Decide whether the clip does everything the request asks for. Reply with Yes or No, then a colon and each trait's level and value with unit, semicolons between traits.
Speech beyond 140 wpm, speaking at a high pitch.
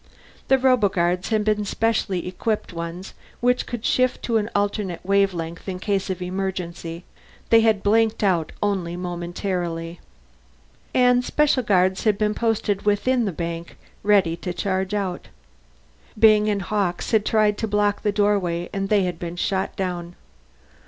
Yes: average, 150 wpm; high, 195 Hz